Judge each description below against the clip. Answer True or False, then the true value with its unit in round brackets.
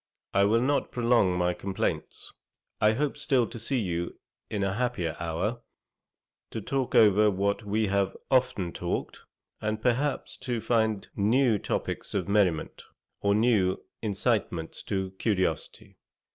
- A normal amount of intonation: True (3.8 semitones)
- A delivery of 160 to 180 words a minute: False (135 wpm)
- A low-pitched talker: True (105 Hz)